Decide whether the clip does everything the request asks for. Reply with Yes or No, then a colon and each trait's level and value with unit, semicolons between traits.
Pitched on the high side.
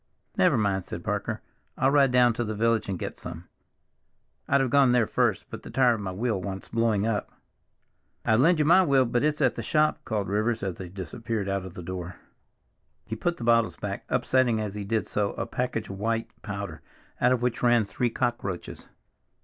No: low, 115 Hz